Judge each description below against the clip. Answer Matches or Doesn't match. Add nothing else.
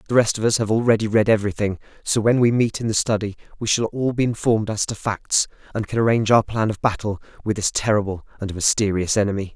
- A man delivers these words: Matches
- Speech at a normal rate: Doesn't match